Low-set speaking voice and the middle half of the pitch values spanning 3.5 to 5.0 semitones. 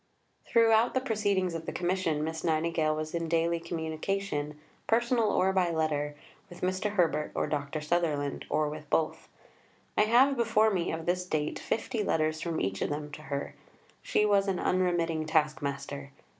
No: medium, 165 Hz; average, 4.0 semitones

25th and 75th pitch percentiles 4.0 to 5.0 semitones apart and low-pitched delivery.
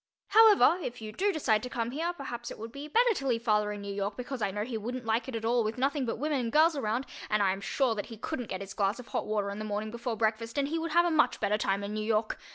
No: average, 4.5 semitones; high, 230 Hz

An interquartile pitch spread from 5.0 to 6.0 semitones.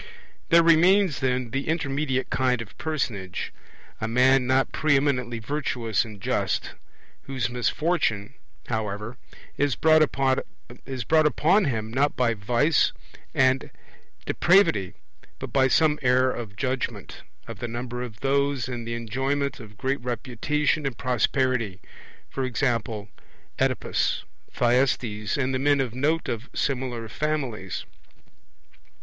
No: average, 3.4 semitones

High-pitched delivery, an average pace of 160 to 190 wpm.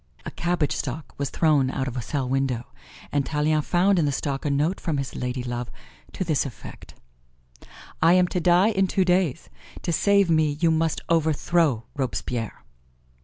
No: medium, 150 Hz; average, 170 wpm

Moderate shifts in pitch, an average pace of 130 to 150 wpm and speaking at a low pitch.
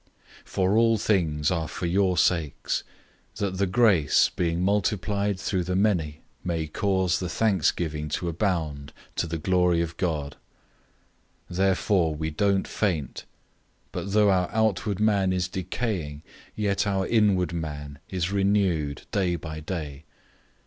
Yes: average, 3.8 semitones; average, 140 wpm; very low, 90 Hz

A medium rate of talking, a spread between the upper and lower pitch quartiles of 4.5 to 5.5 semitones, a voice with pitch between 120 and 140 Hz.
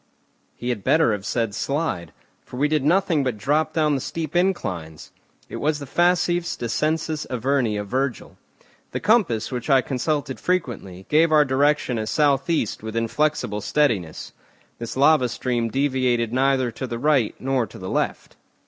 Yes: average, 165 wpm; average, 4.8 semitones; low, 135 Hz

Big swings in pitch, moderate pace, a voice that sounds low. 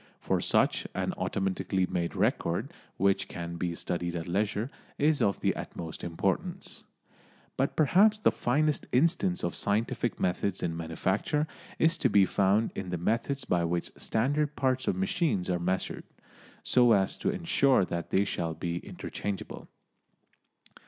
Yes: wide, 8.0 semitones; average, 145 wpm; low, 100 Hz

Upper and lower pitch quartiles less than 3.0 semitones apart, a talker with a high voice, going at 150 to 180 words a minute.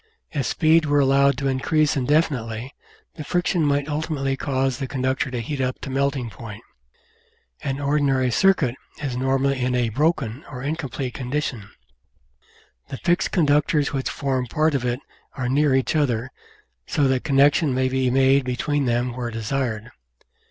No: narrow, 2.4 semitones; low, 135 Hz; average, 155 wpm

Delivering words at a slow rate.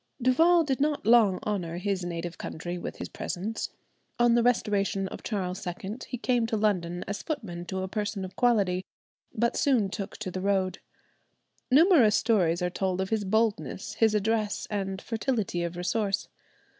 No: average, 170 wpm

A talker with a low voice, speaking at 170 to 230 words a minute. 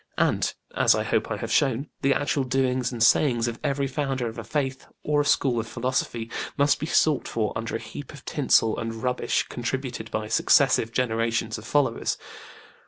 Yes: low, 125 Hz; average, 185 wpm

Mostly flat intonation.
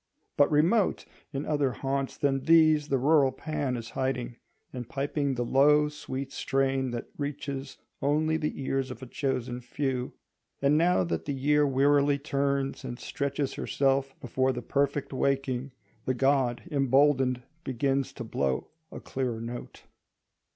Yes: narrow, 1.8 semitones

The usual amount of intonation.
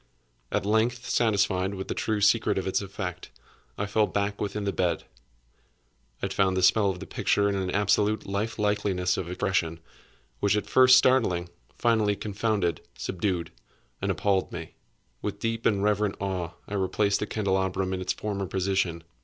No: narrow, 2.0 semitones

